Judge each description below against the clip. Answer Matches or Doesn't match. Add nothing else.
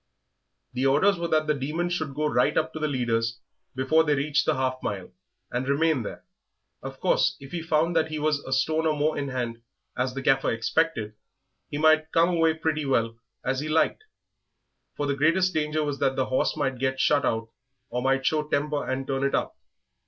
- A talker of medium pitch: Matches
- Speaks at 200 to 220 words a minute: Matches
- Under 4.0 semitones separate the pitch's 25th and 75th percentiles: Matches